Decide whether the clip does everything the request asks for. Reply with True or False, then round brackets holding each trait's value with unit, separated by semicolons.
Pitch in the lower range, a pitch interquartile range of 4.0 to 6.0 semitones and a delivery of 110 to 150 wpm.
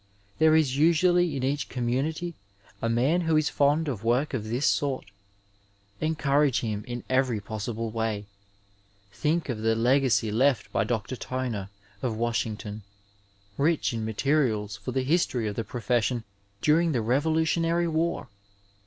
True (130 Hz; 5.3 semitones; 145 wpm)